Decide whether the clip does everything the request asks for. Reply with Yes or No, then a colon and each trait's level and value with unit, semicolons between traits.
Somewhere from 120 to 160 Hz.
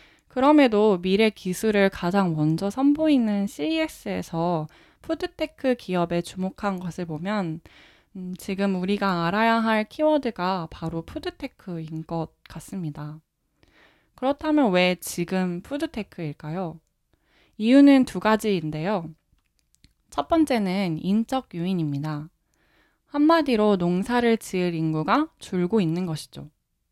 No: high, 190 Hz